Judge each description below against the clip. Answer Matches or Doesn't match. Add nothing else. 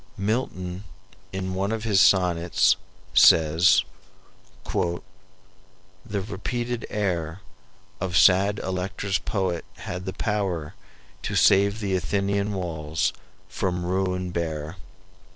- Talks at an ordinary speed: Doesn't match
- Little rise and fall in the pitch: Matches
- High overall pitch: Doesn't match